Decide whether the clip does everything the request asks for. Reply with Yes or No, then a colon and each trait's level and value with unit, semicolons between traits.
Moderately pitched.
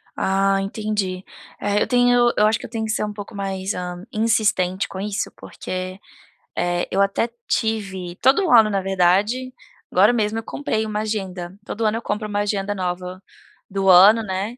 No: high, 205 Hz